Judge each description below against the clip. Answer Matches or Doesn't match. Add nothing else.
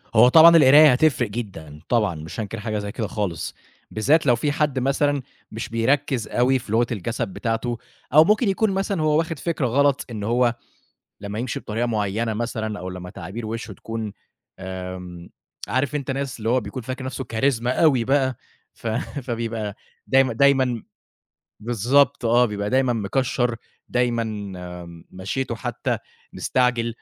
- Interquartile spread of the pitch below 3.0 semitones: Doesn't match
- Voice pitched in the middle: Doesn't match